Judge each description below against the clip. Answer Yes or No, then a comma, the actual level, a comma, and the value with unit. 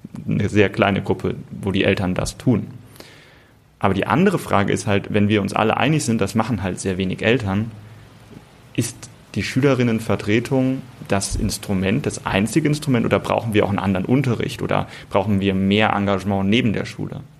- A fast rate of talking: No, average, 170 wpm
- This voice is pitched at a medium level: No, low, 105 Hz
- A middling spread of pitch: Yes, average, 3.5 semitones